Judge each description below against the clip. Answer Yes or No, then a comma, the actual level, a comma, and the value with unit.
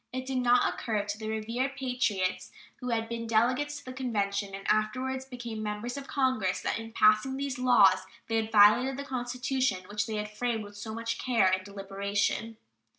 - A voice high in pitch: Yes, high, 225 Hz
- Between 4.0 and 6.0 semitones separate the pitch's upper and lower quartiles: No, average, 3.6 semitones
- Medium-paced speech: Yes, average, 190 wpm